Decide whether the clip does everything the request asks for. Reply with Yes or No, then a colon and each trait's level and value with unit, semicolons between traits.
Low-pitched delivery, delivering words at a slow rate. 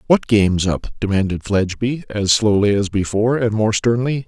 No: low, 105 Hz; average, 170 wpm